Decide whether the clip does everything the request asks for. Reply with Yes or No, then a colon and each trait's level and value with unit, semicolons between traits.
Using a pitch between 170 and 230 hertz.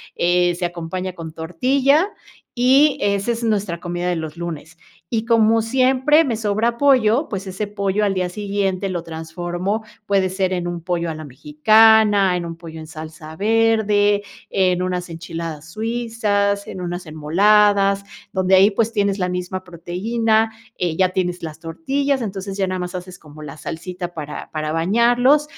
Yes: high, 190 Hz